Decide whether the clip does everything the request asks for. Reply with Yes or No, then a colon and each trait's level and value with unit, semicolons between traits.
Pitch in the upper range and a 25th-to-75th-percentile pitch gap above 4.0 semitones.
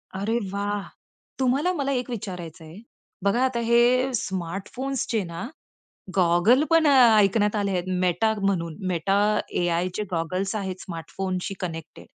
Yes: high, 200 Hz; average, 5.0 semitones